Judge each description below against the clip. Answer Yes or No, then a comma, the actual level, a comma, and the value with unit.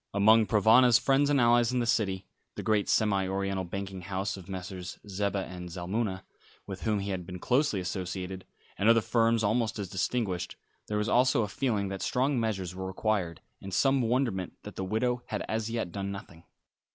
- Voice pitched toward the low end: Yes, low, 100 Hz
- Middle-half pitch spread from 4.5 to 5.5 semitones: No, average, 3.5 semitones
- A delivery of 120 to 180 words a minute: No, average, 190 wpm